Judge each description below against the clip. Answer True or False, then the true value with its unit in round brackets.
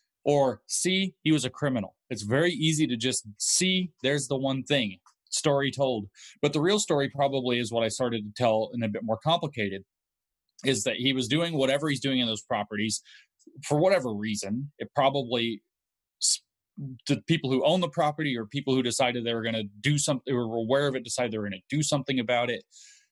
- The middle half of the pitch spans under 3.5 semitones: False (4.0 semitones)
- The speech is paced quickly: True (210 wpm)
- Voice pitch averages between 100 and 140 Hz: True (135 Hz)